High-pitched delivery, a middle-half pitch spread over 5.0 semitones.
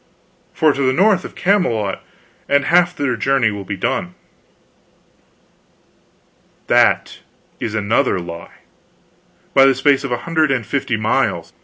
No: low, 135 Hz; wide, 5.5 semitones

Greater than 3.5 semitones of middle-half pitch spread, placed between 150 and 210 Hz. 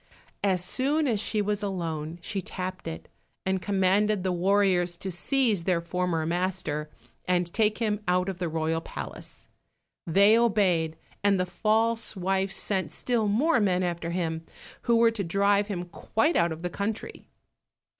No: average, 3.2 semitones; high, 190 Hz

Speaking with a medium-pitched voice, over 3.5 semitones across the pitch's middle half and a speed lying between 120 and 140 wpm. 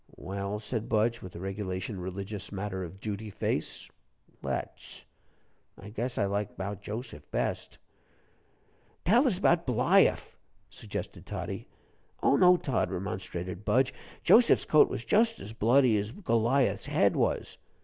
No: low, 105 Hz; average, 5.0 semitones; slow, 135 wpm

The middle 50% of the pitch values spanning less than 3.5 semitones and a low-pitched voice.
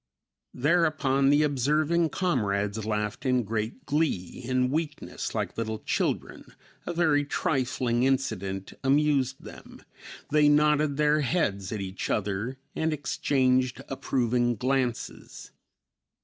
No: average, 4.7 semitones; low, 130 Hz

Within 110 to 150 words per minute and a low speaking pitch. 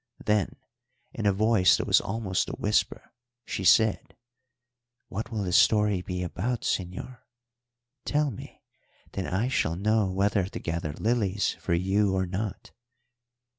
Yes: average, 140 wpm; low, 100 Hz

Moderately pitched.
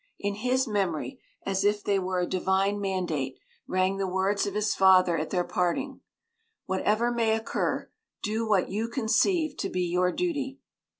No: high, 200 Hz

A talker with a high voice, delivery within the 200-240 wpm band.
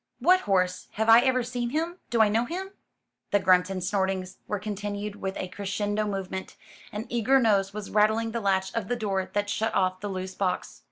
Yes: high, 205 Hz; fast, 205 wpm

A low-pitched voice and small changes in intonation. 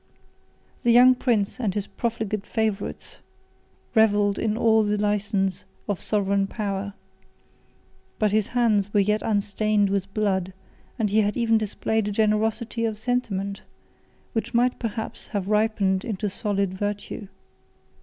No: high, 210 Hz; narrow, 1.8 semitones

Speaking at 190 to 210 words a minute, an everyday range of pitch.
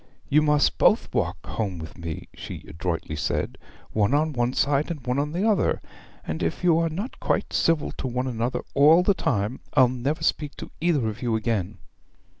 No: average, 195 wpm; wide, 6.1 semitones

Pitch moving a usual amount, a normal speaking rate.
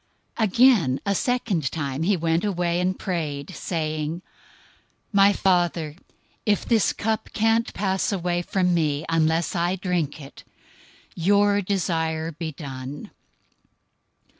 No: average, 4.0 semitones; slow, 120 wpm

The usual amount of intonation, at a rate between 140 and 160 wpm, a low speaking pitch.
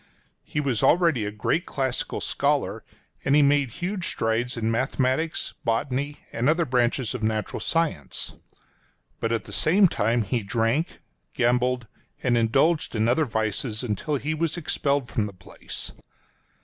Yes: average, 4.7 semitones; average, 150 wpm; low, 125 Hz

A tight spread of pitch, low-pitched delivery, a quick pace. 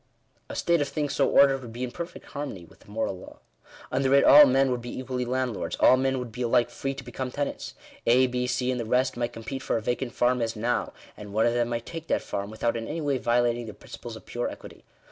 Yes: narrow, 2.2 semitones; low, 125 Hz; fast, 260 wpm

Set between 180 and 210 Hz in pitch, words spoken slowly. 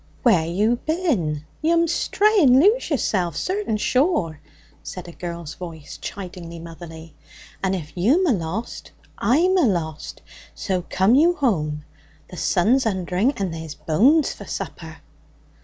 Yes: high, 190 Hz; slow, 130 wpm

